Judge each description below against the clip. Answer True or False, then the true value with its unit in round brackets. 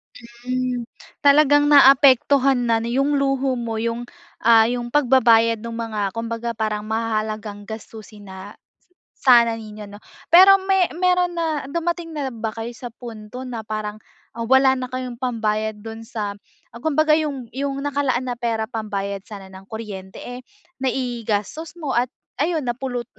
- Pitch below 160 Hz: False (235 Hz)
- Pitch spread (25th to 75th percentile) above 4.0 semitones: False (3.7 semitones)